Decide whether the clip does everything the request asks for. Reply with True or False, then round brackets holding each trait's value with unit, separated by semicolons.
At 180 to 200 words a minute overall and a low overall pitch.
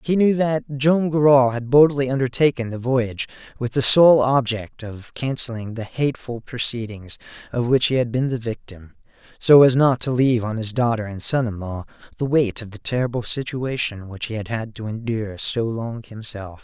True (190 wpm; 120 Hz)